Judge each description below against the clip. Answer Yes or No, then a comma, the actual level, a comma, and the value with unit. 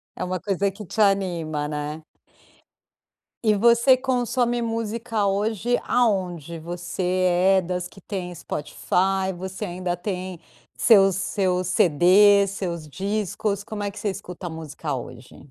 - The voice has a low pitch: No, high, 190 Hz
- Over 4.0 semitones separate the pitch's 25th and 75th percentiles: No, average, 3.2 semitones